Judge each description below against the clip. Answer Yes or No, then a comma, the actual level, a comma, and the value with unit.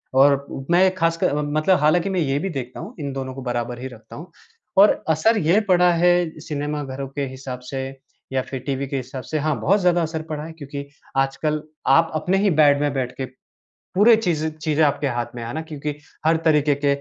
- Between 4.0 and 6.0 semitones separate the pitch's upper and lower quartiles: No, average, 3.5 semitones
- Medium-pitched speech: Yes, medium, 150 Hz